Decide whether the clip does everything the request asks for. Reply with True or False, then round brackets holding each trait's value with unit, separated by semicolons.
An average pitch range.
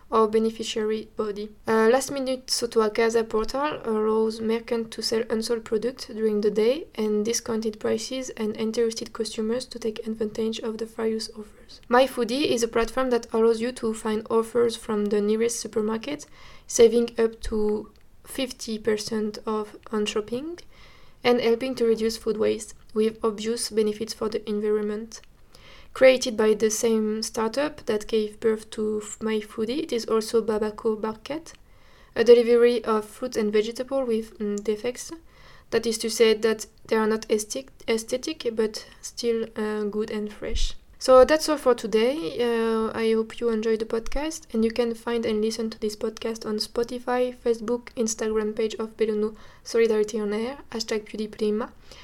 False (1.4 semitones)